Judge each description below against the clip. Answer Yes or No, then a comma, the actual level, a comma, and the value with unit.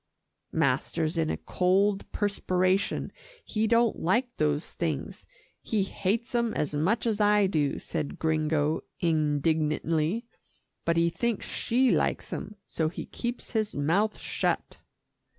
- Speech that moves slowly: Yes, slow, 130 wpm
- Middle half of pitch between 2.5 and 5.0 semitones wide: No, wide, 5.5 semitones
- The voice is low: No, medium, 185 Hz